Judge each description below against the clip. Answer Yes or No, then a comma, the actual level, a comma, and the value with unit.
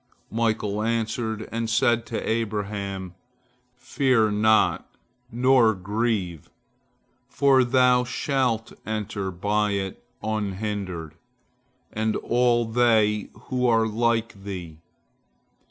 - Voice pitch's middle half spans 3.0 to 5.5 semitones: No, narrow, 2.6 semitones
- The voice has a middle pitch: No, low, 110 Hz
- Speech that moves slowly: Yes, slow, 90 wpm